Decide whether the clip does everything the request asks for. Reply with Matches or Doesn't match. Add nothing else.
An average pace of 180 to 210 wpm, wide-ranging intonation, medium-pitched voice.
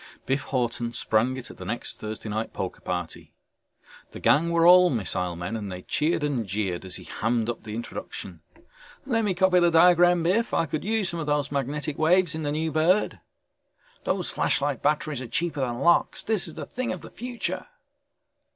Matches